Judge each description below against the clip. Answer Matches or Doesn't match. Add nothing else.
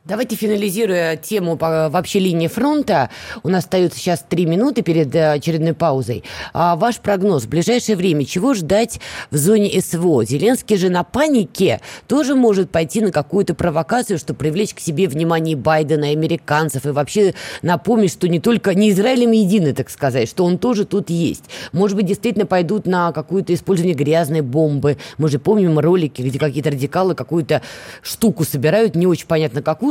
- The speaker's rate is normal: Doesn't match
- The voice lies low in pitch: Doesn't match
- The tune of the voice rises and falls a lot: Doesn't match